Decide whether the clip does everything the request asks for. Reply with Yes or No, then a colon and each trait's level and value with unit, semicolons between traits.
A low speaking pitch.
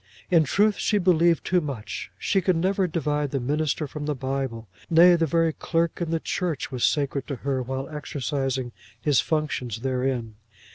No: medium, 150 Hz